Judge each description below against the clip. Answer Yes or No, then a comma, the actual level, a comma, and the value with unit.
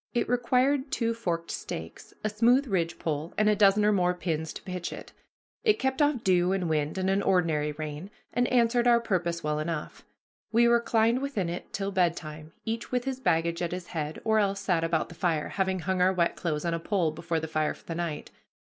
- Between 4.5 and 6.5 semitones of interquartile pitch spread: Yes, wide, 5.6 semitones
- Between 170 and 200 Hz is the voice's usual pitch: Yes, medium, 185 Hz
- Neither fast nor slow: No, fast, 210 wpm